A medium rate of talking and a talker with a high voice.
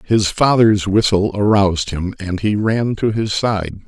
No: average, 170 wpm; low, 100 Hz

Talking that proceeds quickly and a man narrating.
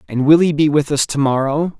Yes: fast, 265 wpm; male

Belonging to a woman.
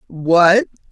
Yes: female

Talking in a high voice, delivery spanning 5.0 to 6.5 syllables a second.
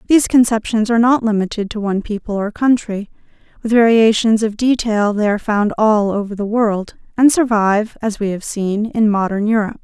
Yes: high, 215 Hz; 5.5 syllables/s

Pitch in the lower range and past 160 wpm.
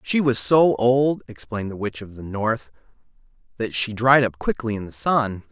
Yes: low, 115 Hz; average, 195 wpm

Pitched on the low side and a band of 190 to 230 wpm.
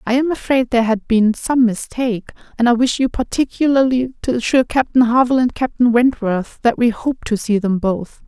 No: high, 240 Hz; average, 195 wpm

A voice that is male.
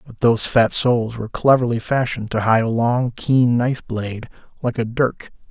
Yes: male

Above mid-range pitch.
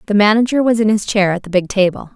Yes: high, 205 Hz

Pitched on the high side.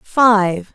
Yes: high, 205 Hz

